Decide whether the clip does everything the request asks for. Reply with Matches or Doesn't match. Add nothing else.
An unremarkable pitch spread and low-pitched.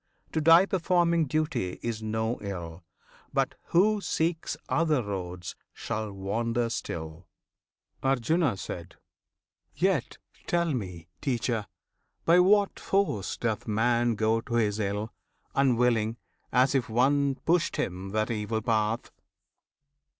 Doesn't match